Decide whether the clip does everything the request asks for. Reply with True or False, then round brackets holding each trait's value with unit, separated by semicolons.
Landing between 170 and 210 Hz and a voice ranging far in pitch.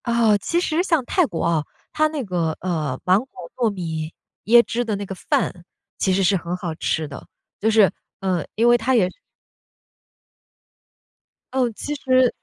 True (205 Hz; 6.0 semitones)